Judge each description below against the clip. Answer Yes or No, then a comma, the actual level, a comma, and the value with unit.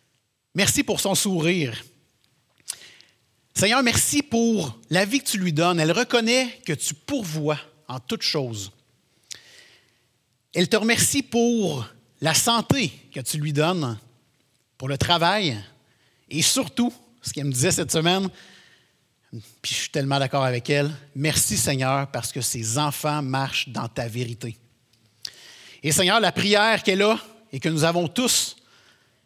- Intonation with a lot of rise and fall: Yes, wide, 7.2 semitones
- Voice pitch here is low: No, medium, 150 Hz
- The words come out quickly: No, slow, 145 wpm